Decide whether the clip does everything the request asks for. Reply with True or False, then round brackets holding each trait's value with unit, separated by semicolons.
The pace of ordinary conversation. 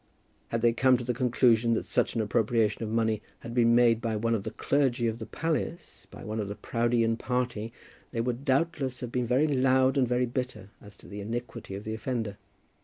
False (215 wpm)